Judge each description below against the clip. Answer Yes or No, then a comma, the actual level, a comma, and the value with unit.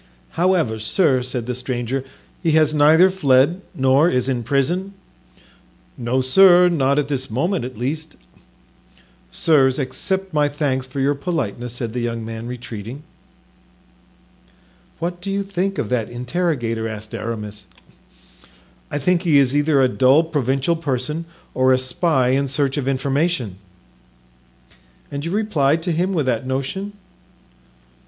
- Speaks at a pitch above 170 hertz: No, low, 135 Hz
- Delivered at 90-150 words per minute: Yes, average, 140 wpm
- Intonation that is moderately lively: Yes, average, 4.8 semitones